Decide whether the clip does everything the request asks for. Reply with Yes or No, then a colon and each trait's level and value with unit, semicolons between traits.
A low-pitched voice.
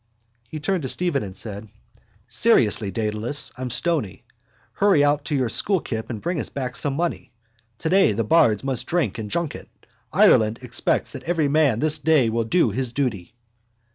Yes: low, 130 Hz